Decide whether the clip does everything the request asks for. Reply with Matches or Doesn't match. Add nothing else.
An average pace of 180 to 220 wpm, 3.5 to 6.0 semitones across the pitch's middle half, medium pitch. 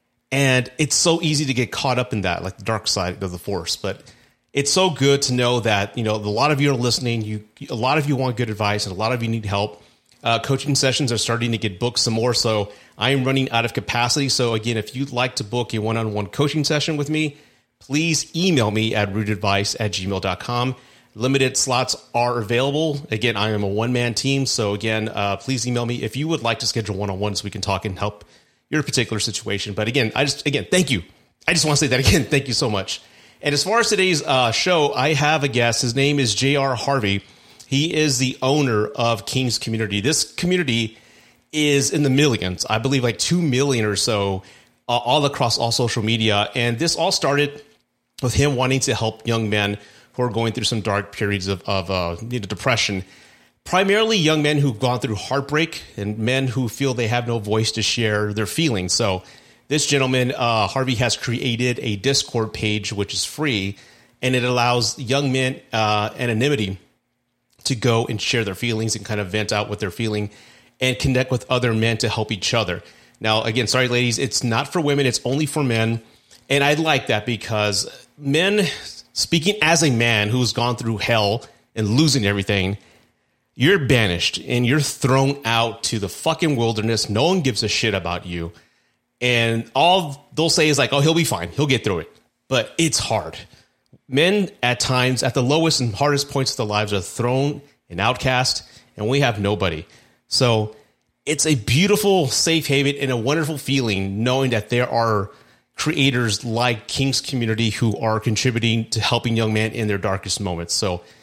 Doesn't match